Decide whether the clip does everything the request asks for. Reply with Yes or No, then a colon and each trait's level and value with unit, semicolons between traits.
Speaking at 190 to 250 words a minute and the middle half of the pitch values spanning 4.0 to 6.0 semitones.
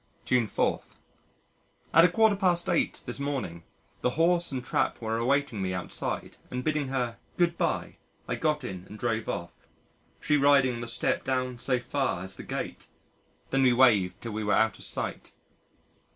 No: average, 175 wpm; average, 4.4 semitones